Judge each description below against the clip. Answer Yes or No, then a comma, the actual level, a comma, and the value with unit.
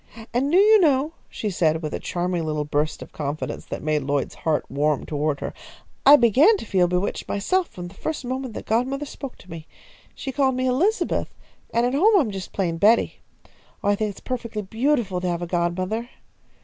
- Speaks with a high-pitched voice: Yes, high, 205 Hz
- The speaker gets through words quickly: Yes, fast, 210 wpm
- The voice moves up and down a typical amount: No, wide, 7.5 semitones